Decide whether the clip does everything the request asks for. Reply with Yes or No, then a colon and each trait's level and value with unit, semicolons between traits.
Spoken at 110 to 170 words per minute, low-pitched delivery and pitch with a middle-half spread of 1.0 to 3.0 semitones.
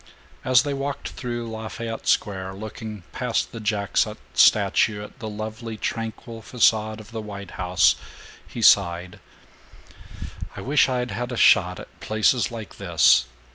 Yes: average, 140 wpm; low, 110 Hz; average, 2.7 semitones